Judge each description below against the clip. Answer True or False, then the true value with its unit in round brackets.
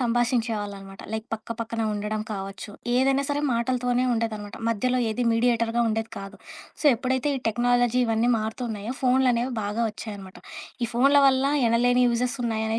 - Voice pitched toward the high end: True (230 Hz)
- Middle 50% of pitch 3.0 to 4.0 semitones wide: False (2.4 semitones)